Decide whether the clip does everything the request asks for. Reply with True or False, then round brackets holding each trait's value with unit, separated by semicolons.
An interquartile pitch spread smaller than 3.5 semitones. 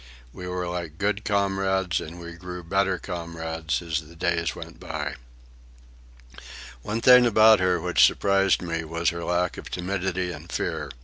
True (2.5 semitones)